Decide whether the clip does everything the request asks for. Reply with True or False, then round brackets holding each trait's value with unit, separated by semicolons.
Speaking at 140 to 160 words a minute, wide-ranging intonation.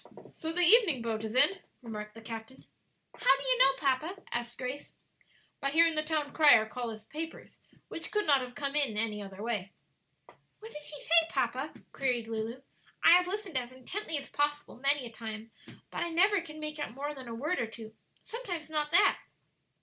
False (195 wpm; 5.8 semitones)